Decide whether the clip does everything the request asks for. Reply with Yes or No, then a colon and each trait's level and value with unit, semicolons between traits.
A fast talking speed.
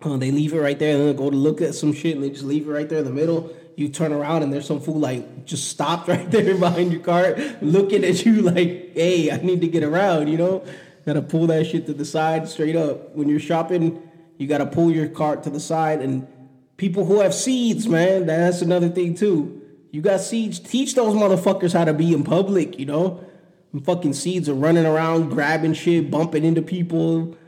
Yes: fast, 230 wpm